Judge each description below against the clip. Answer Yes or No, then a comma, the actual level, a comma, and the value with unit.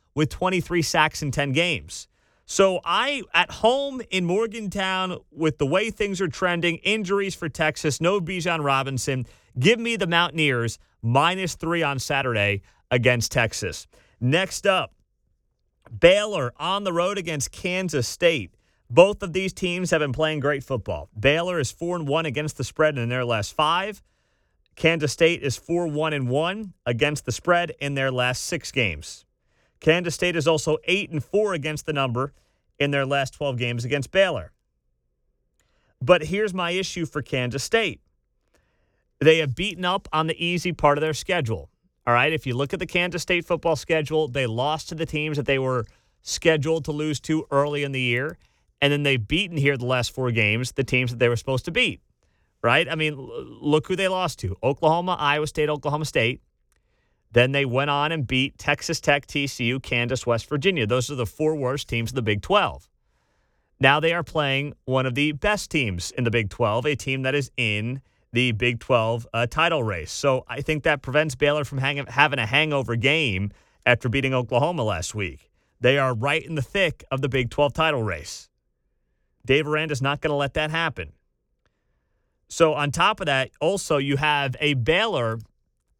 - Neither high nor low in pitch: Yes, medium, 145 Hz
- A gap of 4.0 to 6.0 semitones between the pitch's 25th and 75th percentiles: Yes, average, 4.9 semitones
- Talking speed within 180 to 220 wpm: Yes, average, 185 wpm